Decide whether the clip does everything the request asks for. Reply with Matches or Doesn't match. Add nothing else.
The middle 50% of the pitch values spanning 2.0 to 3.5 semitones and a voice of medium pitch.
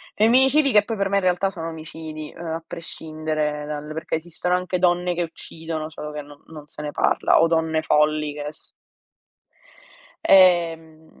Matches